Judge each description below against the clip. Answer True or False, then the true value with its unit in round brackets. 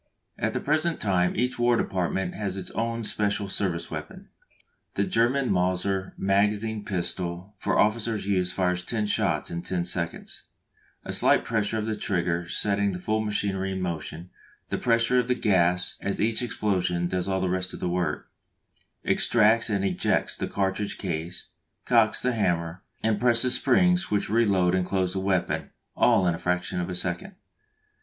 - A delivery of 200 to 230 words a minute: False (165 wpm)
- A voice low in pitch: True (95 Hz)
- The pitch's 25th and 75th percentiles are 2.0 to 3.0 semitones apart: False (3.4 semitones)